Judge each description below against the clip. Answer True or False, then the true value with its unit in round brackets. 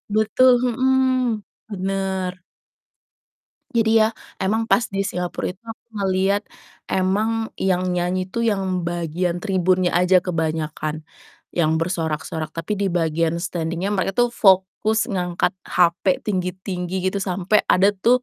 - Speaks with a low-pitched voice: False (185 Hz)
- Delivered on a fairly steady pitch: False (3.1 semitones)